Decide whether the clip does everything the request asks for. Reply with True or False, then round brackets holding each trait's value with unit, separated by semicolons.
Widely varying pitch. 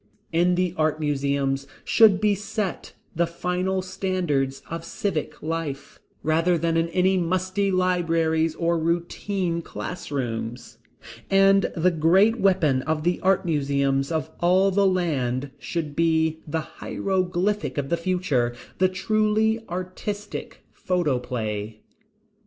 False (3.7 semitones)